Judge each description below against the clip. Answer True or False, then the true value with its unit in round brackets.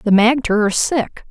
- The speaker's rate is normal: True (185 wpm)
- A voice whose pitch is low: False (230 Hz)